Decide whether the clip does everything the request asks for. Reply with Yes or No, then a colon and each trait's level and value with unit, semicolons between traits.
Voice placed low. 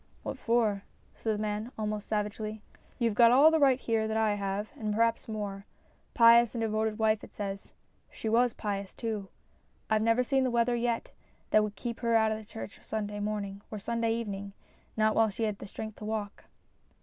No: high, 220 Hz